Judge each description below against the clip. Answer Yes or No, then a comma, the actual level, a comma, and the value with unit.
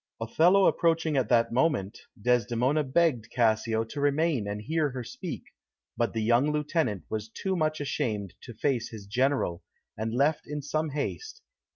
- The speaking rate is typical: Yes, average, 160 wpm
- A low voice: Yes, low, 130 Hz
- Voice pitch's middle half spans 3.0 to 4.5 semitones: No, wide, 5.4 semitones